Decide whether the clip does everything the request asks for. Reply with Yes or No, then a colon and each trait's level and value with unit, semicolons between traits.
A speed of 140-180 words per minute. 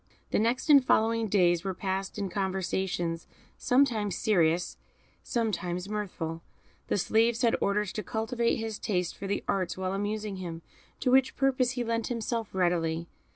Yes: average, 155 wpm